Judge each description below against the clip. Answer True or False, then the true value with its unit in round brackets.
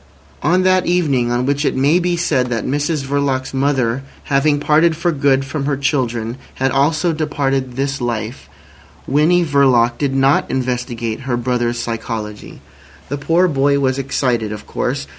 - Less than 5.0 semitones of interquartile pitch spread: True (3.1 semitones)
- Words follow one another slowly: False (160 wpm)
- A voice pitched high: False (135 Hz)